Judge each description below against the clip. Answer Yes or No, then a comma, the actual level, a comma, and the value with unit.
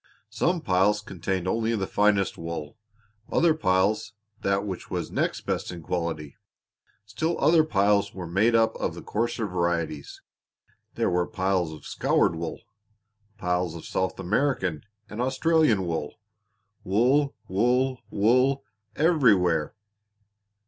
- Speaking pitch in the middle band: No, low, 100 Hz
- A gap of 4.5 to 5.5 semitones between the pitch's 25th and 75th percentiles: Yes, average, 5.1 semitones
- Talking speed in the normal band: No, slow, 125 wpm